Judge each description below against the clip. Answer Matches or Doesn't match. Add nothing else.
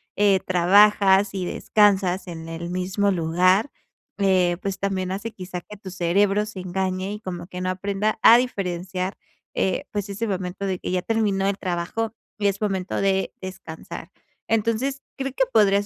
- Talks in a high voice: Matches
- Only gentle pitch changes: Matches